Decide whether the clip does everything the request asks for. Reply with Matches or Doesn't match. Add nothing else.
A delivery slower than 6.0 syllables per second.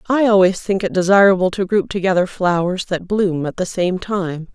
Matches